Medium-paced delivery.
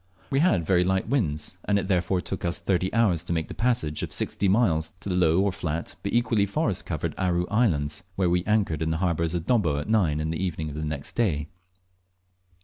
No: fast, 225 wpm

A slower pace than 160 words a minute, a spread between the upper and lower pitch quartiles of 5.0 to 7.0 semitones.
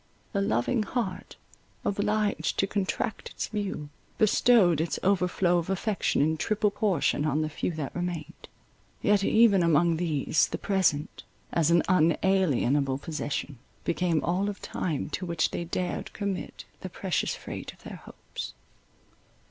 No: average, 140 wpm; average, 4.2 semitones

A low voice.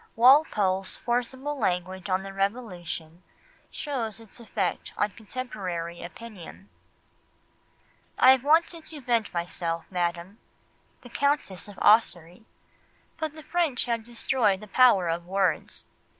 No: high, 210 Hz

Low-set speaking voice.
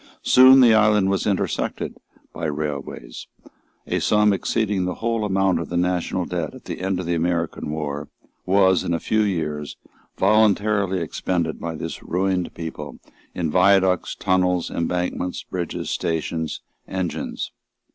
Yes: very low, 90 Hz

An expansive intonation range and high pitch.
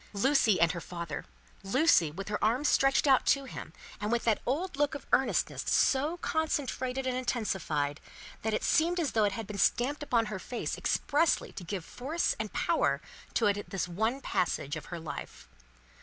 Yes: wide, 6.1 semitones; high, 230 Hz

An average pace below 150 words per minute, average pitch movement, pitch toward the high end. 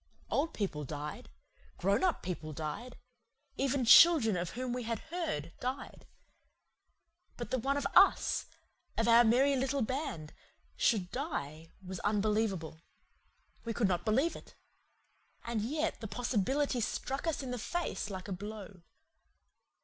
No: average, 140 wpm; wide, 6.2 semitones; high, 230 Hz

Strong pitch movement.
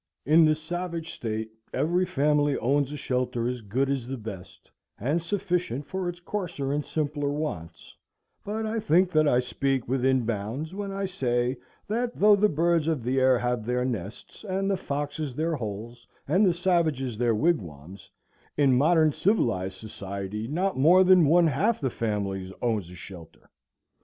Yes: wide, 6.6 semitones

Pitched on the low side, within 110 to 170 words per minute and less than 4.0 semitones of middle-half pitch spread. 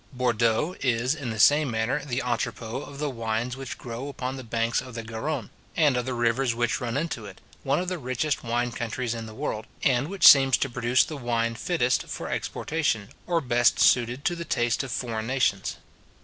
No: low, 125 Hz; fast, 205 wpm; average, 3.1 semitones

